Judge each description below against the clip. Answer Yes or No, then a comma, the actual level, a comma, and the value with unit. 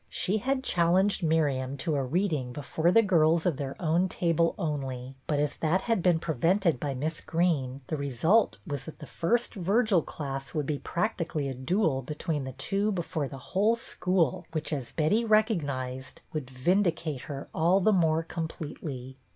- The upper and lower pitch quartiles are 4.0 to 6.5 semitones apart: Yes, average, 4.8 semitones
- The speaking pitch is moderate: Yes, medium, 160 Hz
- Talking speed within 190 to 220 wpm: No, average, 175 wpm